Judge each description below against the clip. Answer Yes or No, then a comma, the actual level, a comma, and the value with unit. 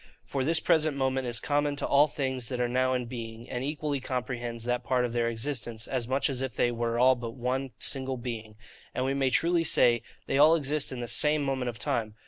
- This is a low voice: Yes, low, 130 Hz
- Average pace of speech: No, fast, 230 wpm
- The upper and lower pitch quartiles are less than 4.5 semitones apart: Yes, narrow, 2.6 semitones